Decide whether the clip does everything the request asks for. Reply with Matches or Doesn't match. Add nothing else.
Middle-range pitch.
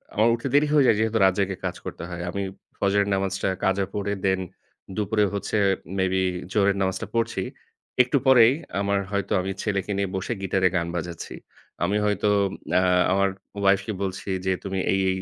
Doesn't match